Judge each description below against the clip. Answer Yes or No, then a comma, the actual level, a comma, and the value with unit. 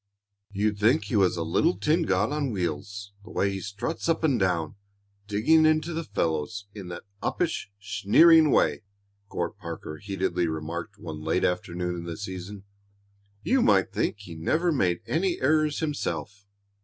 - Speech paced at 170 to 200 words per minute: No, average, 160 wpm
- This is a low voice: Yes, low, 100 Hz